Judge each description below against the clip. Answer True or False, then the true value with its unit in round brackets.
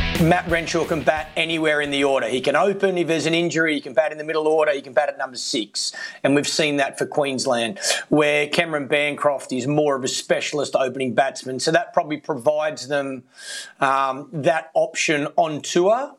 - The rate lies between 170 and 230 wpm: True (200 wpm)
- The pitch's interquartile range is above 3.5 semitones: False (2.7 semitones)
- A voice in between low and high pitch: True (150 Hz)